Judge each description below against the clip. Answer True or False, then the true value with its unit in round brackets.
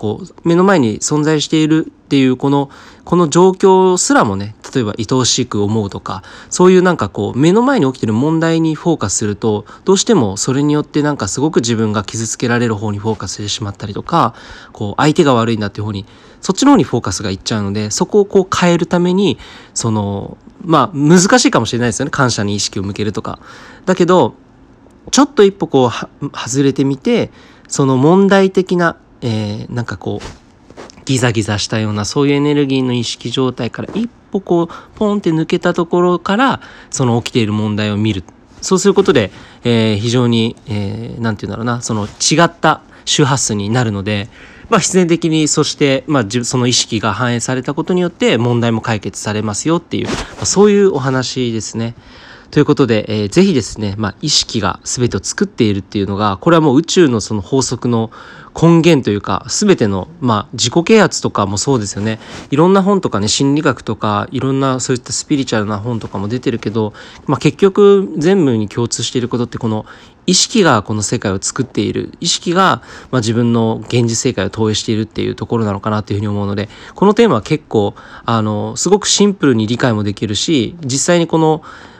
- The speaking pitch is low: True (125 Hz)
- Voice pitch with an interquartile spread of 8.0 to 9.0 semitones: False (6.9 semitones)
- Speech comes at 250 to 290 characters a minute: False (410 characters per minute)